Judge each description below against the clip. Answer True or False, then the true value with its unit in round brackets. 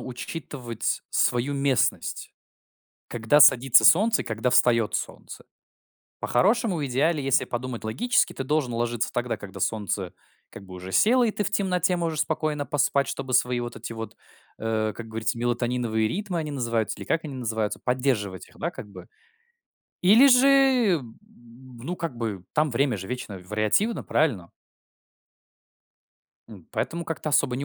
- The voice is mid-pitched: False (125 Hz)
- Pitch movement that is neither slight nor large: False (6.0 semitones)